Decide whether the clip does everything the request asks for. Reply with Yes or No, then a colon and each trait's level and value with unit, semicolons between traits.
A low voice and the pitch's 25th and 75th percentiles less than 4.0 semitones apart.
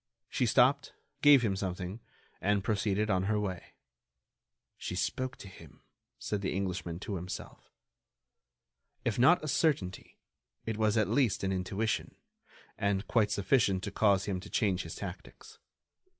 Yes: low, 100 Hz; average, 3.0 semitones